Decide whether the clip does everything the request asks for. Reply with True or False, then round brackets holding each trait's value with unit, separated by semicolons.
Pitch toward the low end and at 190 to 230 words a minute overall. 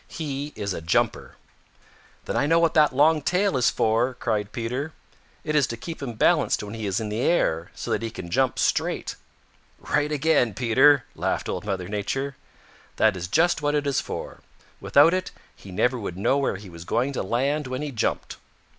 True (130 Hz; 200 wpm)